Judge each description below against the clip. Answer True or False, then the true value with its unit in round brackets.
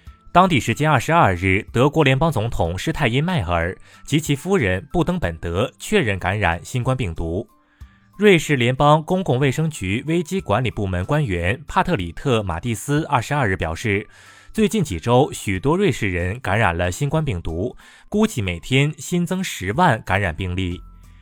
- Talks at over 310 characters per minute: False (265 characters per minute)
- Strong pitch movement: True (8.7 semitones)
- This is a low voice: True (120 Hz)